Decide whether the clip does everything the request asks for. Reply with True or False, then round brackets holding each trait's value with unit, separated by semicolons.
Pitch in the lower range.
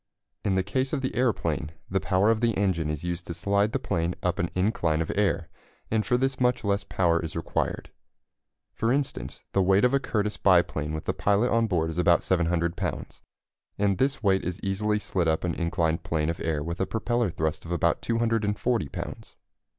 True (95 Hz)